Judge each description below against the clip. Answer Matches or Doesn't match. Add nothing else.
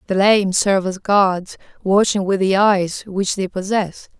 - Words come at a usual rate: Matches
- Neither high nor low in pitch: Doesn't match